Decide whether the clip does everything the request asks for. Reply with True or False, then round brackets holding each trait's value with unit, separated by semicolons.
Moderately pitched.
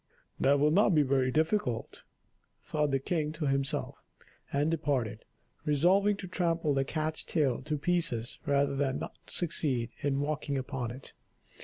True (145 Hz)